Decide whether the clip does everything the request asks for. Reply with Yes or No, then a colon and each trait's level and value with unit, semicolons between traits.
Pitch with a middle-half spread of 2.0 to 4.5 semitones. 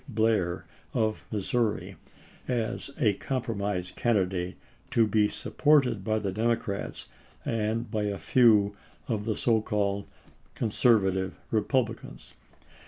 Yes: narrow, 2.5 semitones